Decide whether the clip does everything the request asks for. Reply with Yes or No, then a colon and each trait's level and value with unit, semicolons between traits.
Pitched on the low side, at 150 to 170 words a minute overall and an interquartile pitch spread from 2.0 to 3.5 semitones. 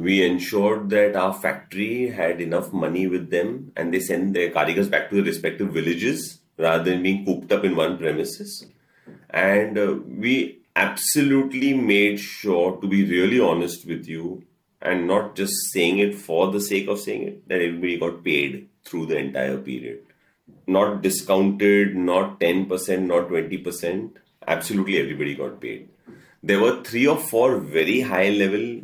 Yes: very low, 95 Hz; average, 160 wpm; narrow, 2.4 semitones